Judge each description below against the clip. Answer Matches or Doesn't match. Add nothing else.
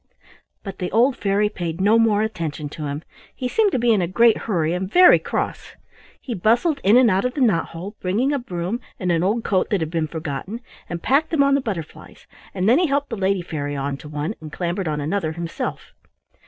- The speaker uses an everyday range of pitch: Doesn't match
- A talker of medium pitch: Doesn't match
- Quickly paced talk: Matches